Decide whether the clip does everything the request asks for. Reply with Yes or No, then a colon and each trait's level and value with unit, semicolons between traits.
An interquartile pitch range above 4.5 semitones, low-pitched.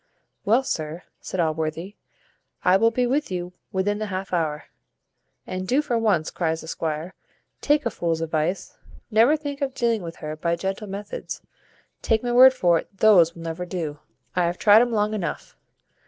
No: wide, 5.5 semitones; medium, 185 Hz